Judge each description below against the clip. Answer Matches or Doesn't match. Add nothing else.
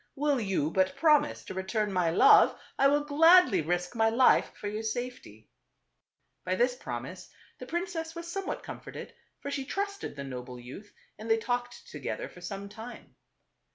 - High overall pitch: Matches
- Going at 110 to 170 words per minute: Doesn't match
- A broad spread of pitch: Matches